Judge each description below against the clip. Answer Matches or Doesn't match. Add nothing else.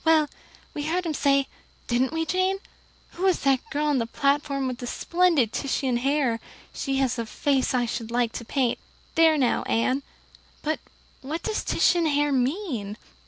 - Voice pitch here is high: Matches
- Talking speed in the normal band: Matches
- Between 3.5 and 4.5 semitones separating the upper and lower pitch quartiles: Matches